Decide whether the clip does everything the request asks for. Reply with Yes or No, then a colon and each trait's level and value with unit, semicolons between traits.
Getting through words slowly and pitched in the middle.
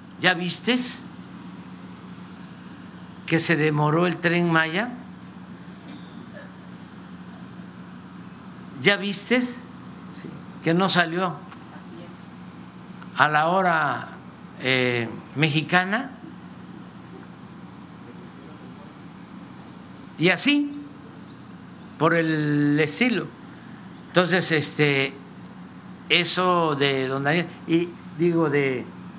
Yes: slow, 65 wpm; medium, 170 Hz